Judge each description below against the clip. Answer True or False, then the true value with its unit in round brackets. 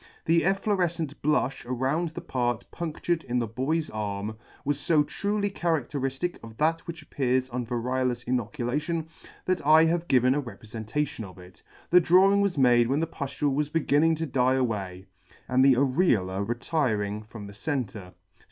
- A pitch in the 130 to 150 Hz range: True (135 Hz)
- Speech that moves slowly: False (160 wpm)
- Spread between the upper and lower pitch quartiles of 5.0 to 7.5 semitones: True (5.3 semitones)